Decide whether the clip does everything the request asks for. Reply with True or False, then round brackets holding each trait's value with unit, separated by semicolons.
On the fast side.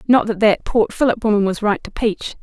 True (245 wpm)